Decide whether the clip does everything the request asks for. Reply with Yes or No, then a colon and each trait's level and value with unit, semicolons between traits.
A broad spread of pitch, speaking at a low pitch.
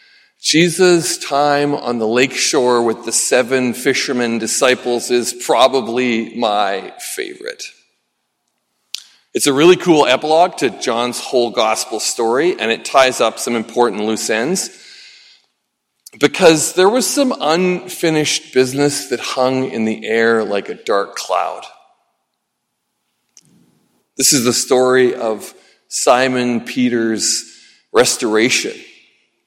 No: average, 4.9 semitones; low, 130 Hz